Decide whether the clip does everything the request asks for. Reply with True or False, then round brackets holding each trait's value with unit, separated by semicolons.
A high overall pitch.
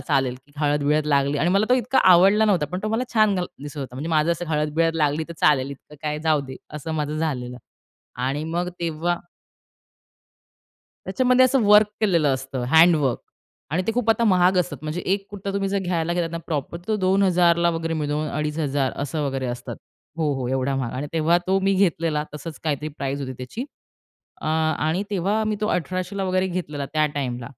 False (160 Hz)